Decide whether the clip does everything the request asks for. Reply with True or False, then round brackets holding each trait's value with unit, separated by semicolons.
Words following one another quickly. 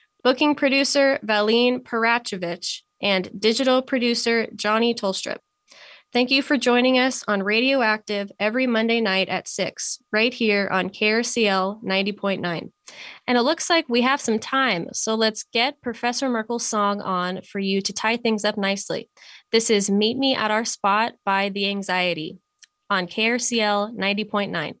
False (150 wpm)